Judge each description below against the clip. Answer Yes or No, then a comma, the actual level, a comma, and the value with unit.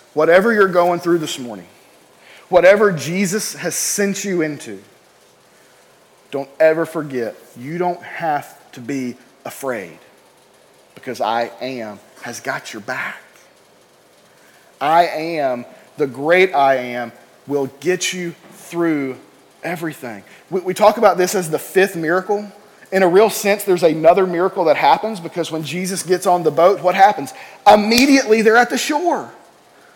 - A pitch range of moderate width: Yes, average, 4.3 semitones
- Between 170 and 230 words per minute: No, average, 140 wpm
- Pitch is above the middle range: No, medium, 175 Hz